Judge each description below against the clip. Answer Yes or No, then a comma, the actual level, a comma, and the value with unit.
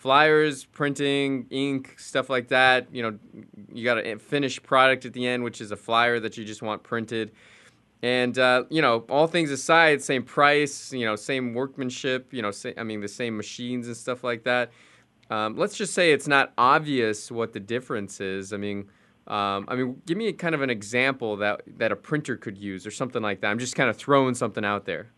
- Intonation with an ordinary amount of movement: Yes, average, 3.5 semitones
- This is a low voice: Yes, low, 125 Hz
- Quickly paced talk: Yes, fast, 215 wpm